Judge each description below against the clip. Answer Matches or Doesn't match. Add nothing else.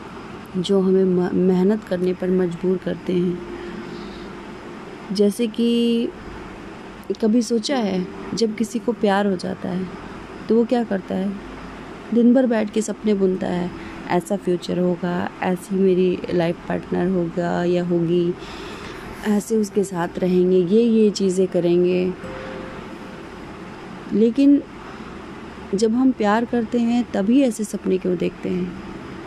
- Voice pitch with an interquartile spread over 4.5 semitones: Doesn't match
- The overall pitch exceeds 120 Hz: Matches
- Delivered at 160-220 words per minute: Doesn't match